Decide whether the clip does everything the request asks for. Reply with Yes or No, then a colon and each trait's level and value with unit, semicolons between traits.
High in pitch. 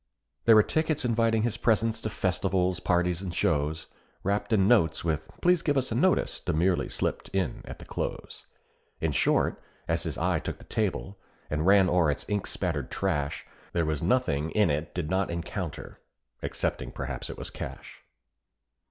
No: very low, 95 Hz